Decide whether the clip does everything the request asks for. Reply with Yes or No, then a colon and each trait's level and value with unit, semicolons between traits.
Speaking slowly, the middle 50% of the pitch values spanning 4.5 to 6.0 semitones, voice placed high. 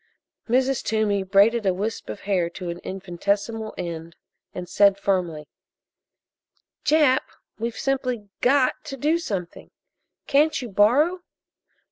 Yes: slow, 120 wpm; wide, 5.6 semitones; high, 210 Hz